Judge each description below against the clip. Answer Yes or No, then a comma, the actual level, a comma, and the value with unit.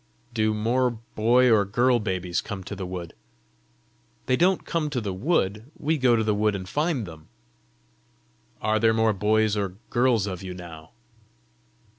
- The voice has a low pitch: Yes, low, 110 Hz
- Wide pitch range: No, average, 4.3 semitones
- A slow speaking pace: No, average, 165 wpm